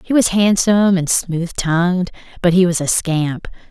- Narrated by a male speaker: No, female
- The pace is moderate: Yes, average, 180 wpm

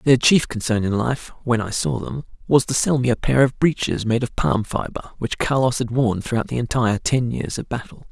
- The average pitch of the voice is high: No, low, 120 Hz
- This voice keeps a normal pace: No, fast, 235 wpm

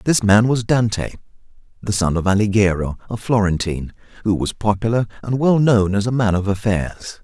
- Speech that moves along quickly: No, average, 175 wpm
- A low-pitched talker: Yes, low, 105 Hz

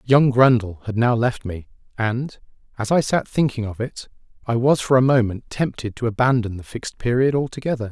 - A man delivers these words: Yes, male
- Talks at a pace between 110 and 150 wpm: No, average, 190 wpm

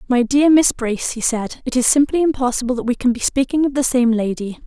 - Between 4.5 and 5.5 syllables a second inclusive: No, 5.9 syllables/s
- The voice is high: Yes, very high, 250 Hz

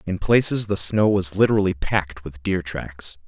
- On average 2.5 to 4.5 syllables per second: No, 4.9 syllables/s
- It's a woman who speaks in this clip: No, male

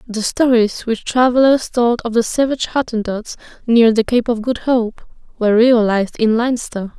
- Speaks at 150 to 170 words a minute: Yes, average, 165 wpm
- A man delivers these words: No, female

